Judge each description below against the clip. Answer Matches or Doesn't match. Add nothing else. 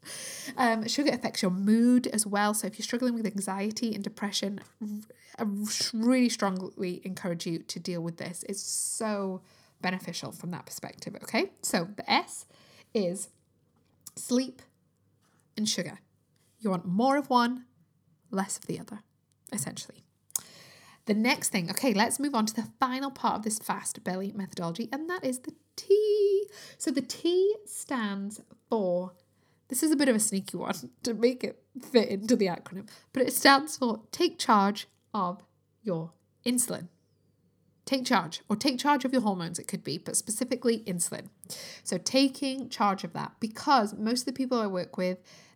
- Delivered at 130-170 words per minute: Matches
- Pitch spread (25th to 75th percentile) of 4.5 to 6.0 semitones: Matches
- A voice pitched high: Matches